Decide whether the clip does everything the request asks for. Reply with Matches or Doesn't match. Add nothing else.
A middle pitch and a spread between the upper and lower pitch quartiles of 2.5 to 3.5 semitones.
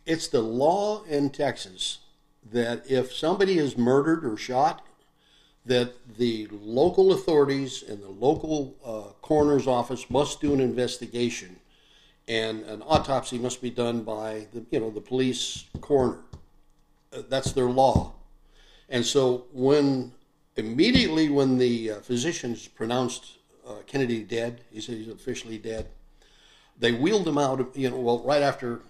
Doesn't match